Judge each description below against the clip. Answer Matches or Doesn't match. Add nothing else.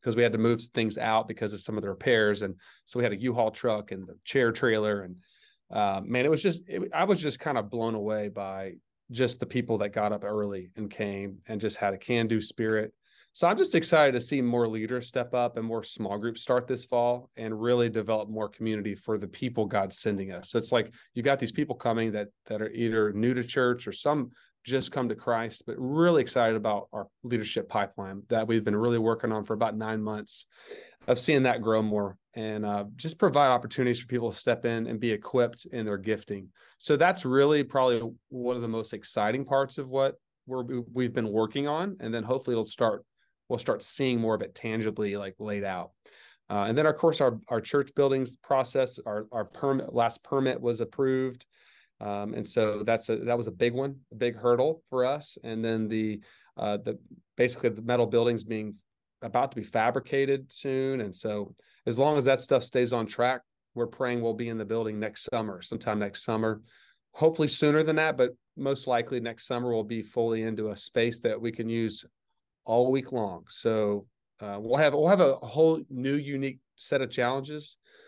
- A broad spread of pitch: Doesn't match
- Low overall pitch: Matches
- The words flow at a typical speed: Doesn't match